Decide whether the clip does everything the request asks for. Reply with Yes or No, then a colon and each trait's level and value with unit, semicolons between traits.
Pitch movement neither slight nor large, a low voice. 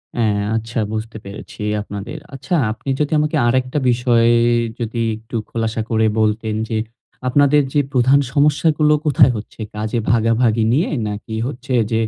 Yes: average, 3.6 semitones; low, 120 Hz